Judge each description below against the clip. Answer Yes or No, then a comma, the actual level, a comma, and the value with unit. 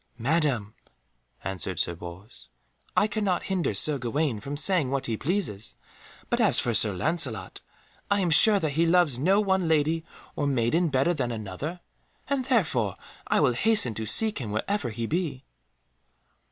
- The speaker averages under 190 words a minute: Yes, average, 160 wpm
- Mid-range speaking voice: Yes, medium, 145 Hz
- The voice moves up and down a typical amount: No, wide, 7.6 semitones